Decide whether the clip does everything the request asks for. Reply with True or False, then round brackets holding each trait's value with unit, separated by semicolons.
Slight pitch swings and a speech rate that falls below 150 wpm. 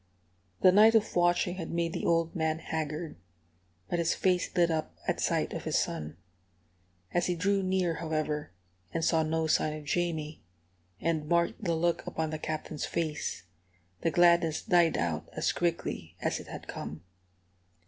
False (2.0 semitones; 165 wpm)